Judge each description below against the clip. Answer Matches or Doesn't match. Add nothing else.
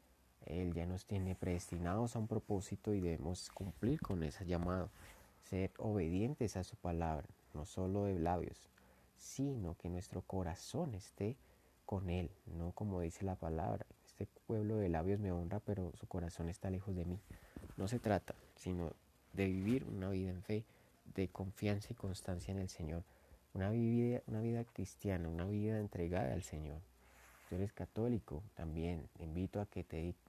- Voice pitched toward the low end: Matches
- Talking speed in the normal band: Matches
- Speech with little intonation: Doesn't match